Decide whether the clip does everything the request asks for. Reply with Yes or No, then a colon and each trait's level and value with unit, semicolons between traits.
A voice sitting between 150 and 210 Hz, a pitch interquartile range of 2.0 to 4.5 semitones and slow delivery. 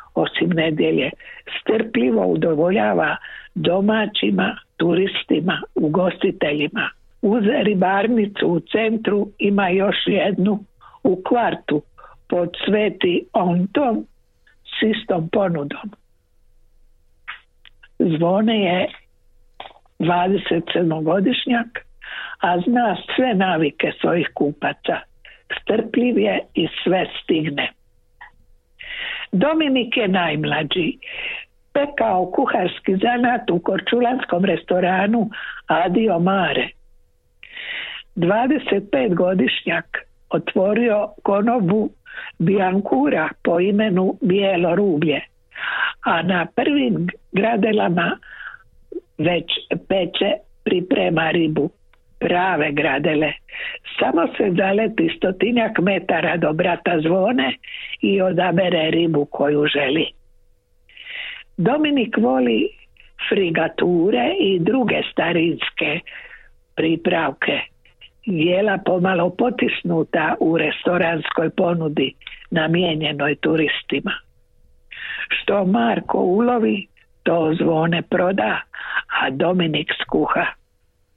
No: high, 190 Hz; average, 5.2 semitones; slow, 75 wpm